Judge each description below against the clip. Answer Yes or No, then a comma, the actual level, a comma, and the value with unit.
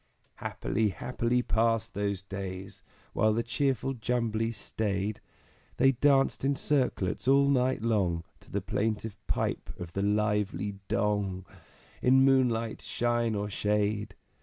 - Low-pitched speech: Yes, low, 110 Hz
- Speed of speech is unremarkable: No, slow, 130 wpm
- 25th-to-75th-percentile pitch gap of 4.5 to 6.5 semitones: No, average, 3.5 semitones